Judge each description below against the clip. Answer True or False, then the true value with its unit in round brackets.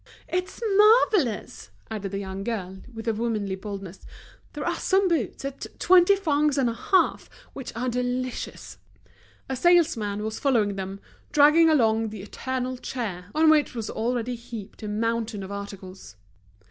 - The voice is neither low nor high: False (230 Hz)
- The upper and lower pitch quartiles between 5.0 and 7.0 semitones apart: True (5.3 semitones)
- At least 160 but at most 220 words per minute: False (150 wpm)